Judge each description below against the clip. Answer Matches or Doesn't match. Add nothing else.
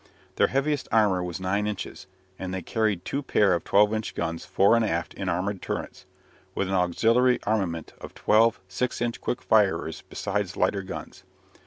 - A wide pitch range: Doesn't match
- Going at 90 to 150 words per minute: Doesn't match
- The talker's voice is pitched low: Matches